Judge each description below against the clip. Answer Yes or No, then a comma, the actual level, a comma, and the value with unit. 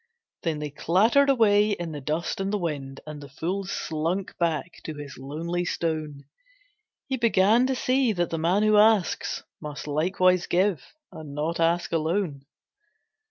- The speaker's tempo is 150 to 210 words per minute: Yes, average, 160 wpm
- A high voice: No, medium, 170 Hz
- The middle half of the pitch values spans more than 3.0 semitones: Yes, average, 4.7 semitones